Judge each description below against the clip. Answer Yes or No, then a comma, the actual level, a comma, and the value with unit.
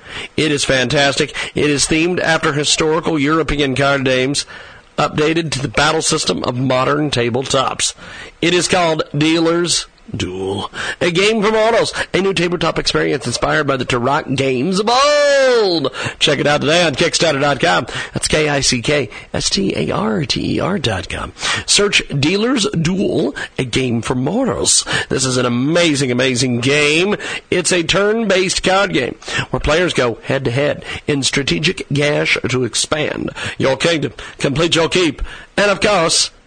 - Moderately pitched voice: Yes, medium, 155 Hz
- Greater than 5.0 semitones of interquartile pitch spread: No, average, 4.4 semitones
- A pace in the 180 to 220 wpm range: No, average, 140 wpm